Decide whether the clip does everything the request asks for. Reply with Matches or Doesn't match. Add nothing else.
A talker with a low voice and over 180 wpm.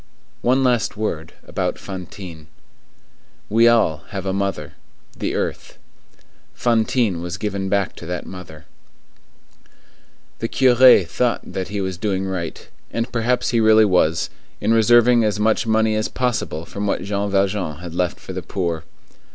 Doesn't match